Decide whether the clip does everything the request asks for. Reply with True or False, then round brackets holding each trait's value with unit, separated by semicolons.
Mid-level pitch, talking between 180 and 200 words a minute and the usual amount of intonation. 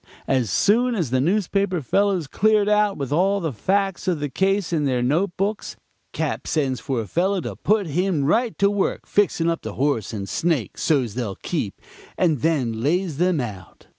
False (170 Hz; 190 wpm; 6.8 semitones)